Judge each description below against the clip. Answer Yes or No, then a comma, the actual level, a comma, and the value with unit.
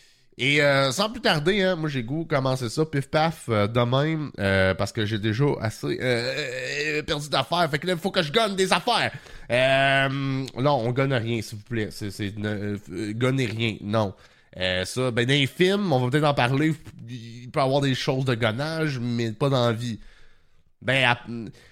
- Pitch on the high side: No, low, 130 Hz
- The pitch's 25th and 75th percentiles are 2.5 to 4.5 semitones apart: No, average, 4.9 semitones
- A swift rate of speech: No, average, 205 wpm